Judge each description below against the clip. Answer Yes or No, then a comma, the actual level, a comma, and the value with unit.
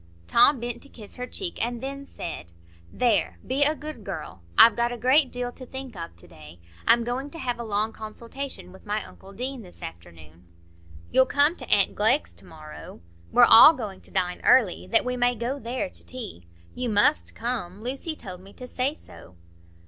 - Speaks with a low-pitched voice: No, high, 235 Hz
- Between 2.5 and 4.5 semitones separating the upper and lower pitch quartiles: No, average, 5.2 semitones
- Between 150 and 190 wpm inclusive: No, average, 200 wpm